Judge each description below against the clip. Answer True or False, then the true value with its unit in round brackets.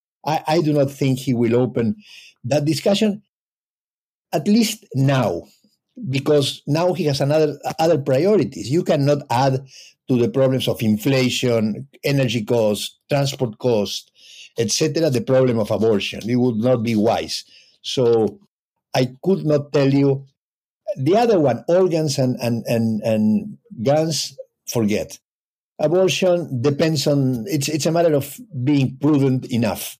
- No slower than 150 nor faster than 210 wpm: False (140 wpm)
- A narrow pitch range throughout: False (4.3 semitones)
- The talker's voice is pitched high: False (135 Hz)